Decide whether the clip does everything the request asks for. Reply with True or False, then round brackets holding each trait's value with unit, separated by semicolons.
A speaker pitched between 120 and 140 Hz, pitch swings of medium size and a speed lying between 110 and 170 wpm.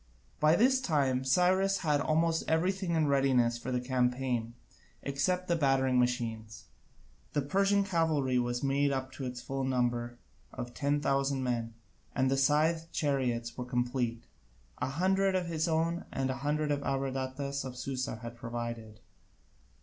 True (135 Hz; 4.2 semitones; 150 wpm)